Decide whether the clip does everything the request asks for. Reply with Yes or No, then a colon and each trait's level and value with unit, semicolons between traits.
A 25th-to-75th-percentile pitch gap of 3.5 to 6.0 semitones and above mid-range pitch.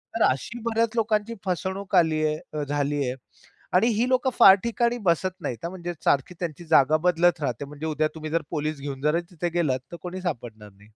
No: average, 4.4 semitones; medium, 165 Hz